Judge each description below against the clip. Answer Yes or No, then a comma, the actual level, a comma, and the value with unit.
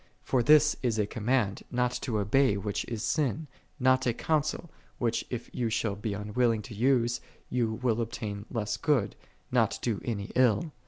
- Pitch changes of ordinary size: Yes, average, 3.3 semitones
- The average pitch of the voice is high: No, low, 115 Hz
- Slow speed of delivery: No, average, 170 wpm